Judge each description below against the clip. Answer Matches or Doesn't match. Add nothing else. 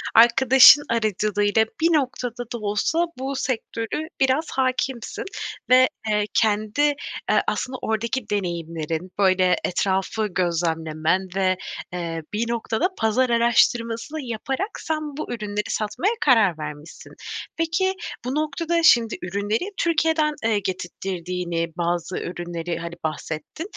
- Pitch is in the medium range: Doesn't match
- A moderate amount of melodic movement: Doesn't match